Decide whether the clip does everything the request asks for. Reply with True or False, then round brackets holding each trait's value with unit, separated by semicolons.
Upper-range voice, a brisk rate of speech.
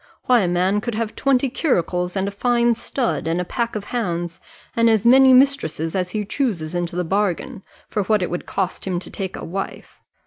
True (200 Hz; 210 wpm)